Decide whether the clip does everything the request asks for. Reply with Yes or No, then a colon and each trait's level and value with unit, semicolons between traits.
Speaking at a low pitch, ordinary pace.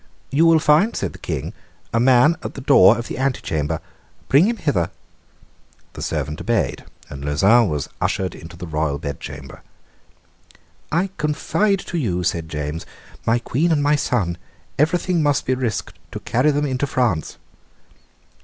Yes: low, 120 Hz; average, 155 wpm